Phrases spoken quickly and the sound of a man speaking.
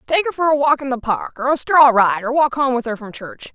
No: fast, 320 wpm; female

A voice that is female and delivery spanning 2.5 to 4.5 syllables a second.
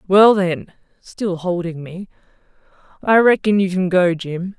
Yes: female; 4.1 syllables/s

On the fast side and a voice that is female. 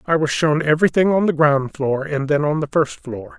No: fast, 250 wpm; male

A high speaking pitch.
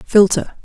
Yes: high, 205 Hz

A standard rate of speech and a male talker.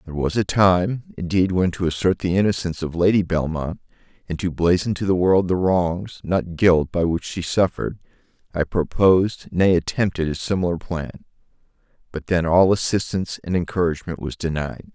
Yes: average, 170 wpm; male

